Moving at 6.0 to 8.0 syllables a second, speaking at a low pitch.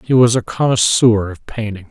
No: 5.0 syllables/s; low, 115 Hz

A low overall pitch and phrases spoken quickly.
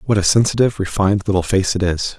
Yes: low, 100 Hz; fast, 220 wpm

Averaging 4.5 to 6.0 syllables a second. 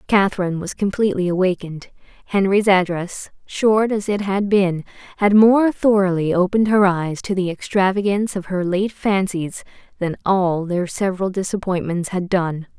Yes: 5.0 syllables/s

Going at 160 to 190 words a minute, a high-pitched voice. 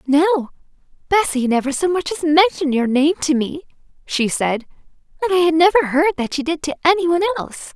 Yes: average, 180 wpm; very high, 315 Hz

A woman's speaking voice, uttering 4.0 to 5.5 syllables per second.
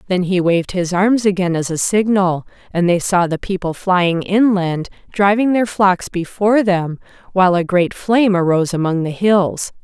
Yes: female; 4.8 syllables/s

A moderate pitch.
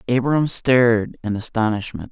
No: low, 115 Hz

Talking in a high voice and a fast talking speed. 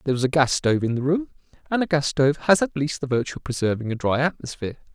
No: medium, 145 Hz; fast, 265 wpm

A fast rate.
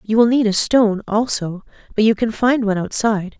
Yes: fast, 210 wpm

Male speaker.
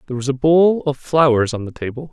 Yes: male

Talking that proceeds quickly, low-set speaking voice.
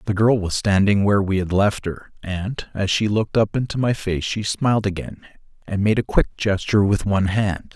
Yes: fast, 215 wpm; low, 100 Hz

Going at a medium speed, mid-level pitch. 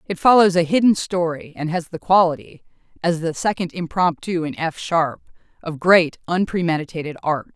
Yes: average, 145 wpm; medium, 170 Hz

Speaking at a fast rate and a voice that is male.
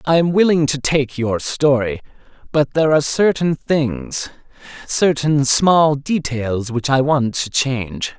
No: average, 145 wpm; male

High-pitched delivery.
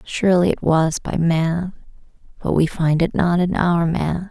No: medium, 170 Hz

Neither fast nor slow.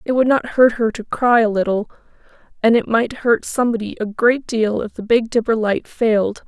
No: fast, 215 wpm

